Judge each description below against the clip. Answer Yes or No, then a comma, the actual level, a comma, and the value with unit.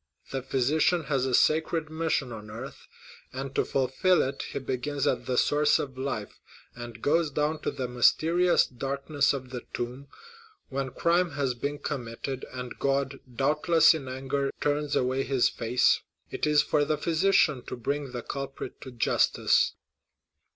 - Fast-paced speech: No, average, 160 wpm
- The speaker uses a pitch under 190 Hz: Yes, low, 135 Hz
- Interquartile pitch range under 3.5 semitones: Yes, average, 2.8 semitones